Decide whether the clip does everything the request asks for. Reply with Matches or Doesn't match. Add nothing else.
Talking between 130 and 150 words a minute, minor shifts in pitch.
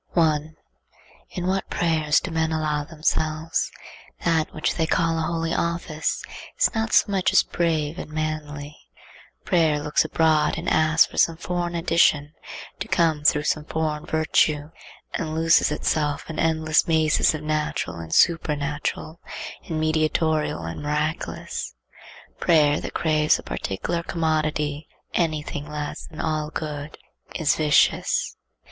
Matches